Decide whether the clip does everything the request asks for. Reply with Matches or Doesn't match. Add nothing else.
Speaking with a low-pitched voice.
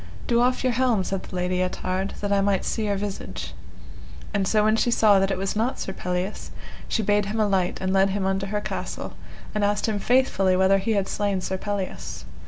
Doesn't match